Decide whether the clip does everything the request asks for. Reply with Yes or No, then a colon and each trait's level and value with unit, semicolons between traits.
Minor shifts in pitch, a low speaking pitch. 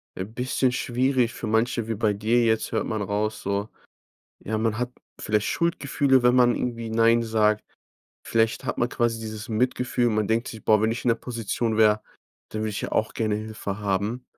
Yes: narrow, 2.0 semitones; low, 110 Hz